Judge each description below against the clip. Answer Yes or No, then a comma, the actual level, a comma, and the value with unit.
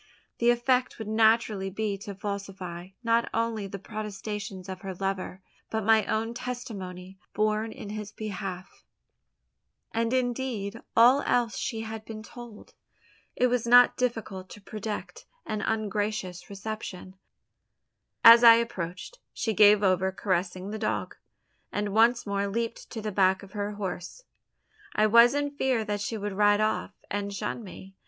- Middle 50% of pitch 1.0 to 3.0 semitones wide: Yes, average, 2.7 semitones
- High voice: Yes, high, 215 Hz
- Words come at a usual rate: Yes, average, 150 wpm